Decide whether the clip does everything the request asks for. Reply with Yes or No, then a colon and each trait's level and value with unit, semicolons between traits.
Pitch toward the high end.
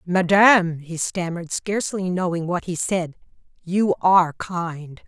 No: medium, 180 Hz